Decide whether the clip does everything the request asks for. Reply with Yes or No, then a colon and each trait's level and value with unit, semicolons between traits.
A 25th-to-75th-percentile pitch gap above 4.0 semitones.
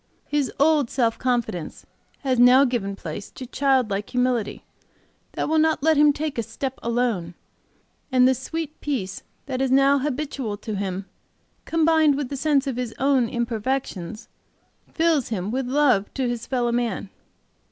No: average, 3.7 semitones